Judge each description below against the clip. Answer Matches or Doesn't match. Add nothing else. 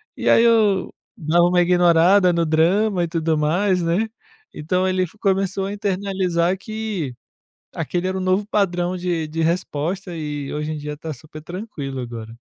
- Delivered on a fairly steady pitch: Doesn't match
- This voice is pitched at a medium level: Matches